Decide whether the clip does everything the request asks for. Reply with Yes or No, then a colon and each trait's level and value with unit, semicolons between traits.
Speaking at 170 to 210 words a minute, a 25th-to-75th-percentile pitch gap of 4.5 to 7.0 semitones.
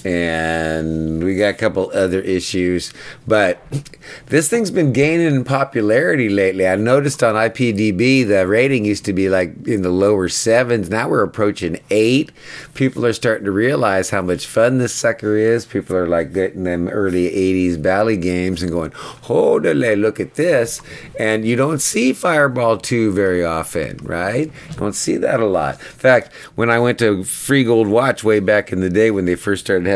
Yes: average, 185 wpm; average, 5.0 semitones